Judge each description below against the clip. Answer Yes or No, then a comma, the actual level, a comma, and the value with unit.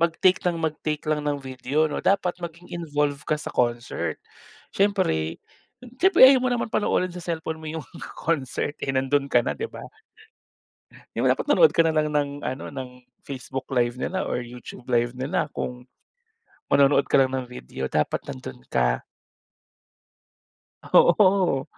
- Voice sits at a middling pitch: Yes, medium, 145 Hz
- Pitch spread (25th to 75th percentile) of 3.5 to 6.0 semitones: Yes, average, 5.1 semitones